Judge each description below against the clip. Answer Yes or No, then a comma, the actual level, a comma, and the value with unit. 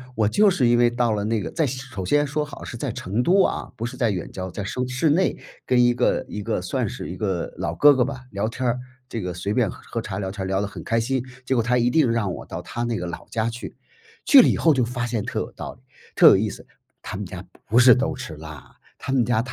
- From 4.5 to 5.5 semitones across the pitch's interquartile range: No, average, 3.7 semitones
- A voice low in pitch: Yes, low, 120 Hz